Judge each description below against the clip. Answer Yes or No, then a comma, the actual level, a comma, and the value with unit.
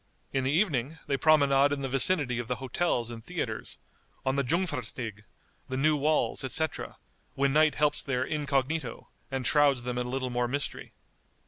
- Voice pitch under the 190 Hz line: Yes, low, 135 Hz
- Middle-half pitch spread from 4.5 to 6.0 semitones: No, average, 3.1 semitones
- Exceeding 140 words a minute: Yes, average, 175 wpm